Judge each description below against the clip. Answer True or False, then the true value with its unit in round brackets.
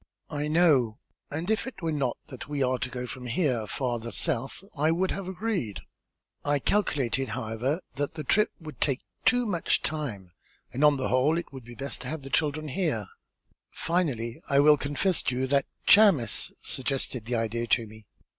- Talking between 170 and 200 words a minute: True (185 wpm)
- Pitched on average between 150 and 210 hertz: False (140 Hz)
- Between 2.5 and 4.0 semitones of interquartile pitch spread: False (4.6 semitones)